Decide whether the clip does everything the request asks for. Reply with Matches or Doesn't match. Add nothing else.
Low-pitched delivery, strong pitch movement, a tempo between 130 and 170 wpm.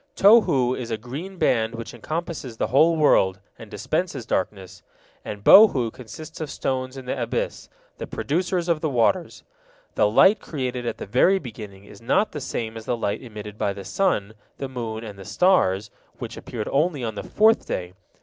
Doesn't match